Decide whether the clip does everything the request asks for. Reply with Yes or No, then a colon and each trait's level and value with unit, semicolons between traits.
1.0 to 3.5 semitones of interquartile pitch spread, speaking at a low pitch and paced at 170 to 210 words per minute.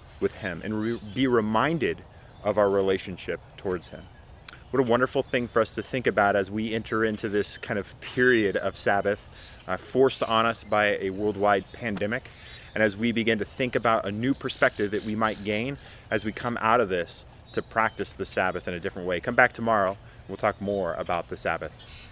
Yes: average, 2.7 semitones; low, 110 Hz; fast, 205 wpm